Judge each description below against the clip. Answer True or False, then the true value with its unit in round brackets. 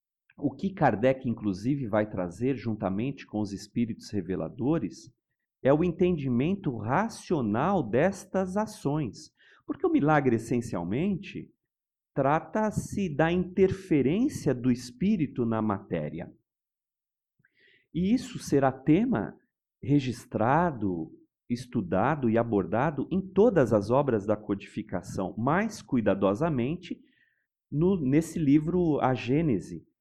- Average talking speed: False (100 wpm)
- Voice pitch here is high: False (140 Hz)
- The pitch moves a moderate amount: False (7.9 semitones)